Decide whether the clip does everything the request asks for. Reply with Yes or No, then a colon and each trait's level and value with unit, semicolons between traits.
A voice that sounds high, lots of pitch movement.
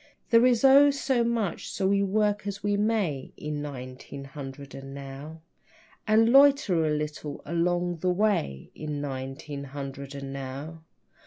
No: medium, 160 Hz; wide, 7.0 semitones